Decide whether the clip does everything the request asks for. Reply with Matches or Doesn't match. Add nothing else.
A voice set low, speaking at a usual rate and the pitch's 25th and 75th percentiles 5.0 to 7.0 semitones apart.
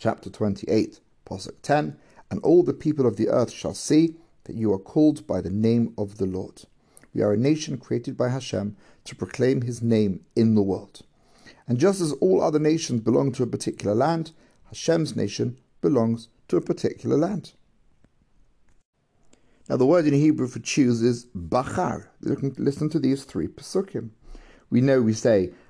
Matches